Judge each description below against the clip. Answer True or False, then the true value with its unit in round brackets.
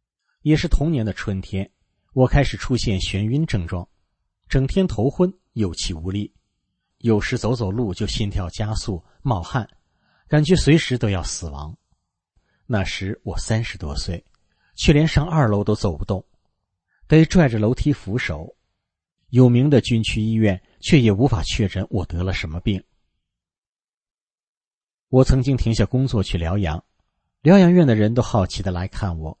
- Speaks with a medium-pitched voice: False (105 Hz)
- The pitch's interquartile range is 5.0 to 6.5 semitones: True (5.4 semitones)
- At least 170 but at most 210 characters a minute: False (220 characters per minute)